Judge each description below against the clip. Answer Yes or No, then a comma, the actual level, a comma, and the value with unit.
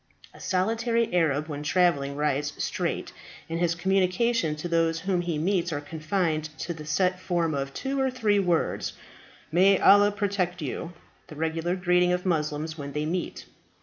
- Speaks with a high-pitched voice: No, medium, 175 Hz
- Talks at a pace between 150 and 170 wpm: Yes, average, 165 wpm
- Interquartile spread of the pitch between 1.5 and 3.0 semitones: No, average, 3.5 semitones